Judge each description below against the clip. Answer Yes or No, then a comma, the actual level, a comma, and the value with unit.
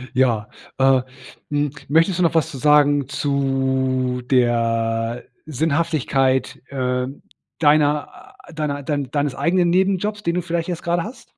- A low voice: No, medium, 145 Hz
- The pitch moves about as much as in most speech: Yes, average, 4.1 semitones